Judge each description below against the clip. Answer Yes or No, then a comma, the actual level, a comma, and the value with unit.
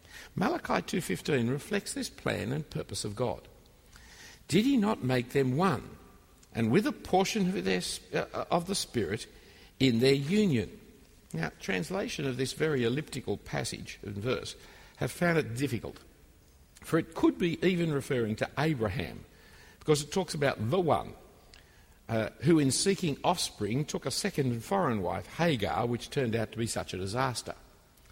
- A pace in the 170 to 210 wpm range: No, average, 160 wpm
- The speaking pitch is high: No, low, 135 Hz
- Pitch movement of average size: No, wide, 7.2 semitones